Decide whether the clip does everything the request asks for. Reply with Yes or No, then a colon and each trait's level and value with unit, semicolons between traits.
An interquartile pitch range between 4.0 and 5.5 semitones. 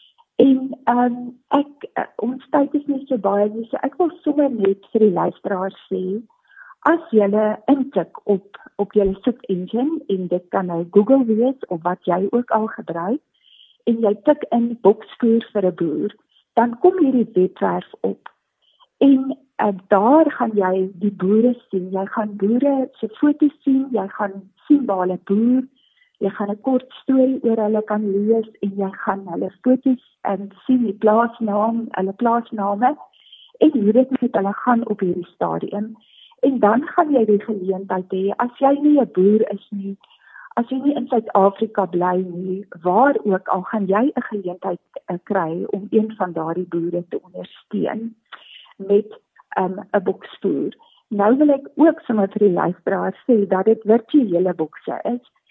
Yes: average, 5.0 semitones